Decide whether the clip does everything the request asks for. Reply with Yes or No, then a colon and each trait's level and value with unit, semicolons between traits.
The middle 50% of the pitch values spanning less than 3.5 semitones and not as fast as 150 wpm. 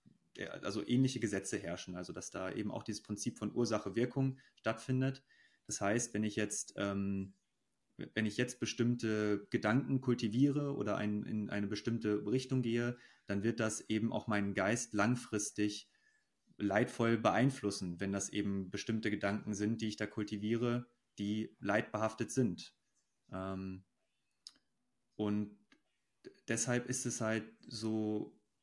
Yes: narrow, 2.6 semitones; average, 135 wpm